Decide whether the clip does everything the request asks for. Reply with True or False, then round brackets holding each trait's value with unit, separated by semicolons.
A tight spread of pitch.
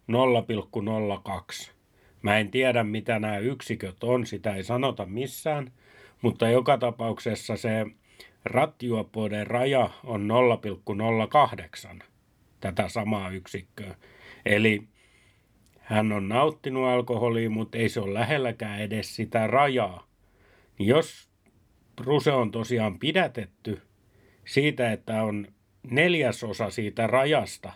False (3.1 semitones)